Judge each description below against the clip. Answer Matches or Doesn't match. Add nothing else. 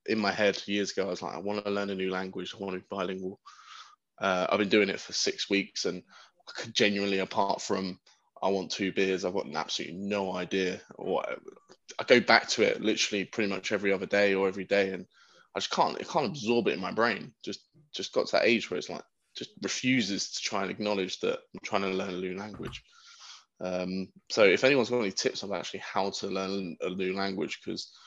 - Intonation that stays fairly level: Matches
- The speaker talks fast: Matches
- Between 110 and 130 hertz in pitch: Doesn't match